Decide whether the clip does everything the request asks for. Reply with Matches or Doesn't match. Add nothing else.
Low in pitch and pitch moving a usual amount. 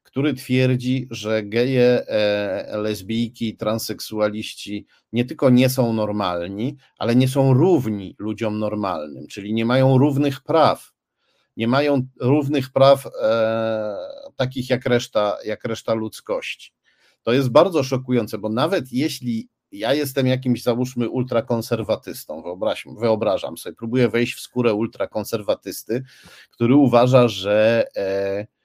Matches